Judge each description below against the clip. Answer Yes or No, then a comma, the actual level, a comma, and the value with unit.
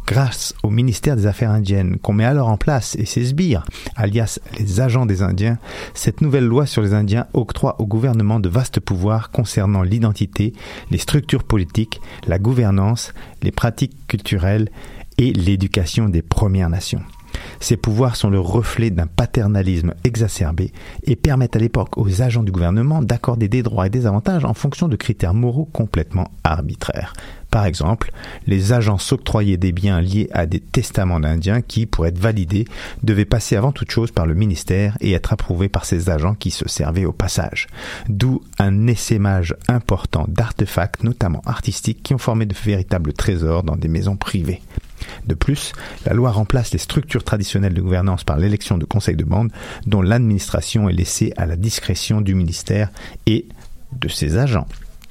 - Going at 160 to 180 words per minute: Yes, average, 170 wpm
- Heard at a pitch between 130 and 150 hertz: No, low, 105 Hz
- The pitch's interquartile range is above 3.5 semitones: Yes, average, 3.9 semitones